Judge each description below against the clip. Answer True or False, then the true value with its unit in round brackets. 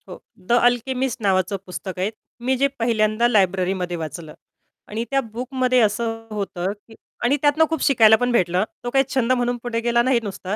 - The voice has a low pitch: False (230 Hz)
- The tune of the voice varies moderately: True (4.2 semitones)